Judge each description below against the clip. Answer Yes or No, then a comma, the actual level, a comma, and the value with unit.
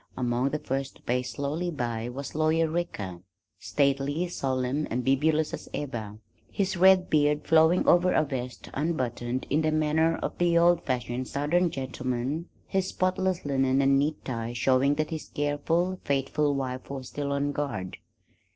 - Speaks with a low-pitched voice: No, medium, 145 Hz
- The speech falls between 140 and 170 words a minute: Yes, average, 160 wpm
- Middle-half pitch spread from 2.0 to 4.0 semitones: Yes, average, 3.7 semitones